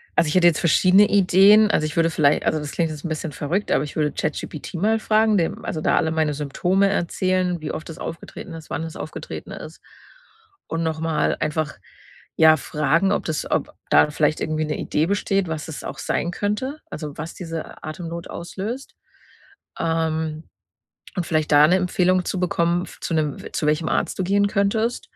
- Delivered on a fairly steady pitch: No, average, 3.2 semitones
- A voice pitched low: No, medium, 165 Hz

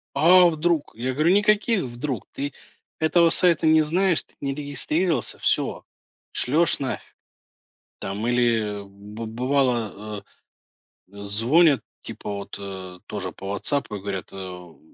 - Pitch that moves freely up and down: Yes, wide, 7.5 semitones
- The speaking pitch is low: Yes, low, 130 Hz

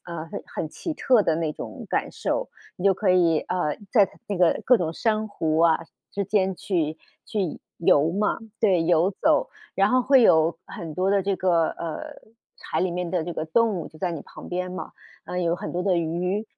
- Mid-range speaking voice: Yes, medium, 180 Hz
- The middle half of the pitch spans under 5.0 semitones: Yes, average, 3.3 semitones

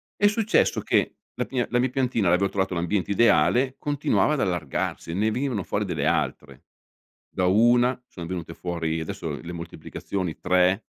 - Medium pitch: No, very low, 95 Hz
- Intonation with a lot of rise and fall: Yes, wide, 6.0 semitones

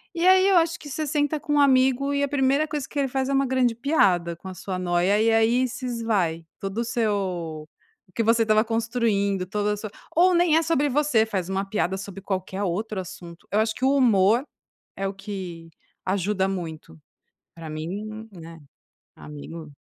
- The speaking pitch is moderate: No, high, 215 Hz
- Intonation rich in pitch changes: Yes, wide, 5.9 semitones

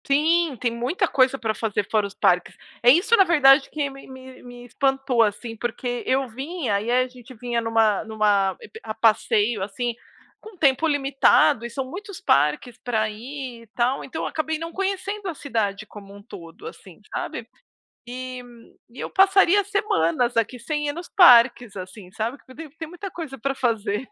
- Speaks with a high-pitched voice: Yes, very high, 250 Hz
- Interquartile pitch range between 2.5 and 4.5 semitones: No, average, 5.0 semitones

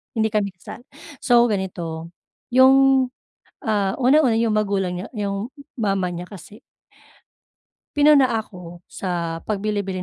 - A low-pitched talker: No, high, 205 Hz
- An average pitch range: Yes, average, 4.5 semitones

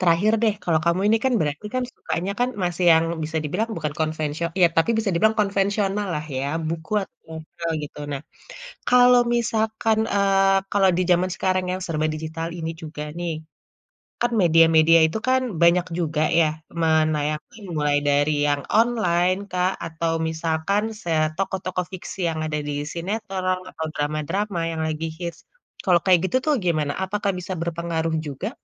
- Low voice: No, medium, 170 Hz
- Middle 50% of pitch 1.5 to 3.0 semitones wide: No, average, 3.7 semitones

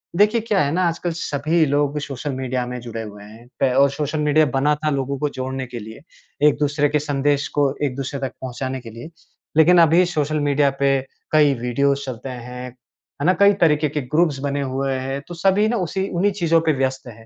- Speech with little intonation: No, average, 3.2 semitones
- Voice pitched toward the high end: No, medium, 140 Hz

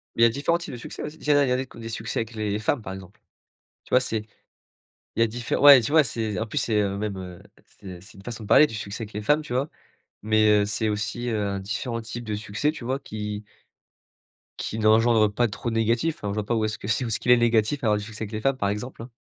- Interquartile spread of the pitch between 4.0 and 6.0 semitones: No, narrow, 2.6 semitones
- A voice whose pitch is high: No, low, 110 Hz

